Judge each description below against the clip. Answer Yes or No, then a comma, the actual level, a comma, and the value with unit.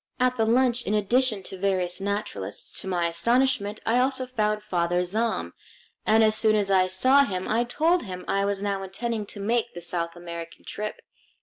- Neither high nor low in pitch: No, high, 210 Hz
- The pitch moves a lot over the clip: No, average, 4.1 semitones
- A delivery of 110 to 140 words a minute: No, average, 190 wpm